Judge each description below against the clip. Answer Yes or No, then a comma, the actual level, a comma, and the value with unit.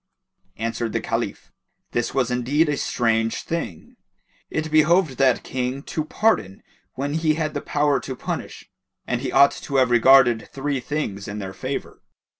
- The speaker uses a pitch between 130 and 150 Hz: Yes, low, 135 Hz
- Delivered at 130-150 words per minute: No, average, 160 wpm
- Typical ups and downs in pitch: Yes, average, 3.9 semitones